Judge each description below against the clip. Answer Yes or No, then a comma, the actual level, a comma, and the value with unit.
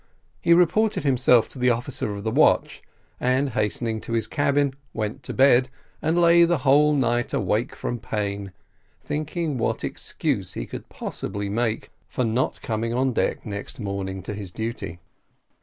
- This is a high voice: No, low, 120 Hz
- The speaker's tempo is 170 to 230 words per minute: No, average, 160 wpm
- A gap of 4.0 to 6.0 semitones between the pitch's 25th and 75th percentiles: Yes, average, 4.8 semitones